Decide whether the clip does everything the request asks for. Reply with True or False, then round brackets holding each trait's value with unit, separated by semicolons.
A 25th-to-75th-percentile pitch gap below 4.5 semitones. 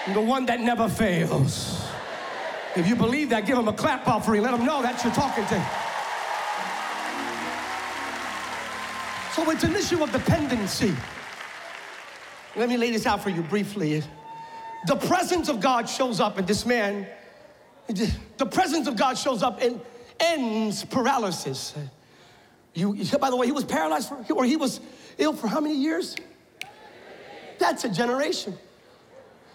False (5.3 semitones)